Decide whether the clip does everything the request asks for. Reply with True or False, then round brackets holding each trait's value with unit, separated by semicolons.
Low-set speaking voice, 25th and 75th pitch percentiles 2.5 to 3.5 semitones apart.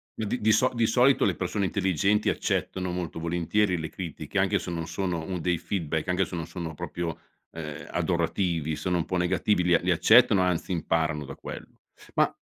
True (90 Hz; 2.9 semitones)